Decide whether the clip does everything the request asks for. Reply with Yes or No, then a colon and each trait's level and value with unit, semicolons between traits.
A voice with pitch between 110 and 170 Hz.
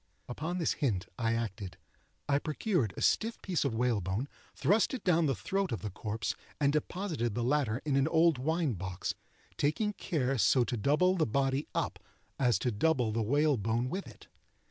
Yes: low, 135 Hz